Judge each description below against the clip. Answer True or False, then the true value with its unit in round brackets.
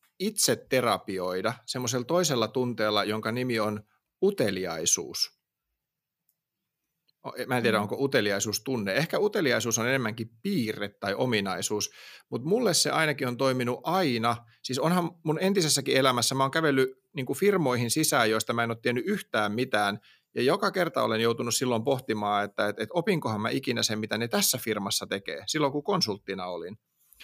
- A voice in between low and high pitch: False (125 Hz)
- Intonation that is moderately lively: False (5.7 semitones)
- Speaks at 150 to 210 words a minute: True (155 wpm)